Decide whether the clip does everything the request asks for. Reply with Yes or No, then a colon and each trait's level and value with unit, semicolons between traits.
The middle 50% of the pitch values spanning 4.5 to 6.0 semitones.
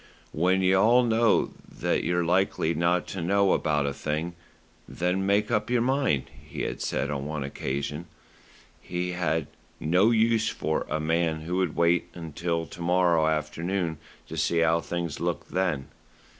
No: average, 3.2 semitones